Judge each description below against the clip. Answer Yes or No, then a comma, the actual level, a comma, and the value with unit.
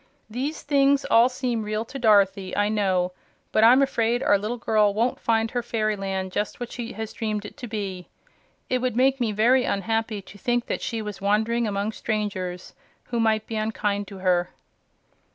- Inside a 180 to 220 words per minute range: Yes, average, 185 wpm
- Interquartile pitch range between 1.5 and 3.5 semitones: Yes, average, 2.8 semitones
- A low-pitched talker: No, high, 220 Hz